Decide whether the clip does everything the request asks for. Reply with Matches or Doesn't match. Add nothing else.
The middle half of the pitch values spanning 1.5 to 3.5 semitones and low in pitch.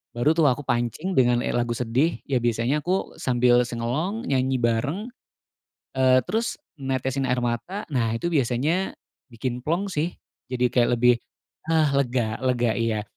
Doesn't match